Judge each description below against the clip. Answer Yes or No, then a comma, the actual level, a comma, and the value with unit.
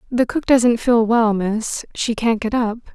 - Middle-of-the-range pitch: No, high, 230 Hz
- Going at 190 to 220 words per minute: Yes, fast, 205 wpm